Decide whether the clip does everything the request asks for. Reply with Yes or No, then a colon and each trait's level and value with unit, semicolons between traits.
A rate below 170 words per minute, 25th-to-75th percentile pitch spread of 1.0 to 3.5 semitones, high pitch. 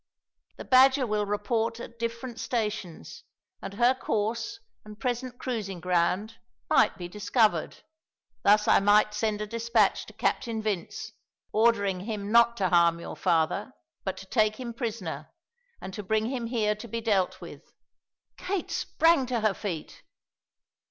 Yes: average, 150 wpm; average, 2.9 semitones; high, 215 Hz